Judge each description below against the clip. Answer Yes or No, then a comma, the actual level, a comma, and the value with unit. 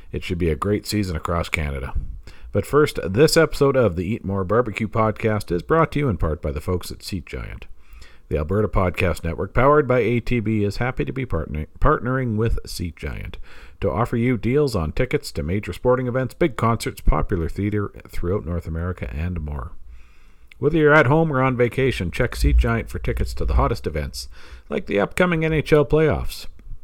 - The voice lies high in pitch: No, low, 100 Hz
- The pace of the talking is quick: No, average, 190 wpm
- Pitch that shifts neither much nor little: No, wide, 7.3 semitones